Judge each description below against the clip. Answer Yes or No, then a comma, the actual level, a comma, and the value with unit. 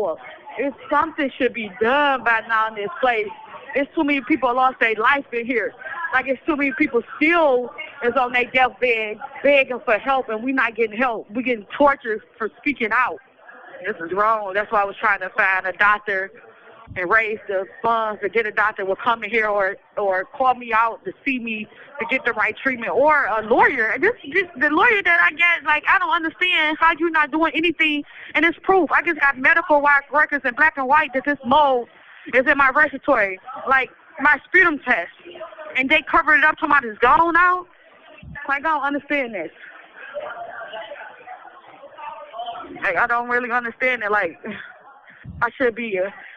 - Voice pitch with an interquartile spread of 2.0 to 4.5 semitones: No, average, 5.0 semitones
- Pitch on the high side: Yes, very high, 265 Hz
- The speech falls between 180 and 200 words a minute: Yes, average, 190 wpm